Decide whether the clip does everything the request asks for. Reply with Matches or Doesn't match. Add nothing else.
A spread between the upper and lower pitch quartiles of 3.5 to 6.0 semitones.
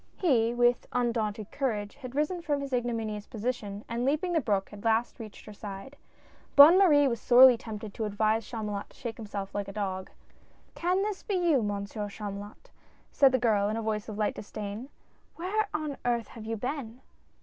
Matches